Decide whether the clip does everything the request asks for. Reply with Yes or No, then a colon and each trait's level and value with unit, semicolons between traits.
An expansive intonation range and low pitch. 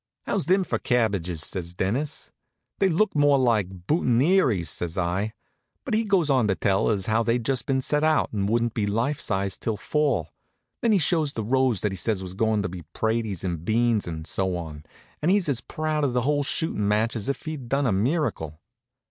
Yes: wide, 6.9 semitones; low, 115 Hz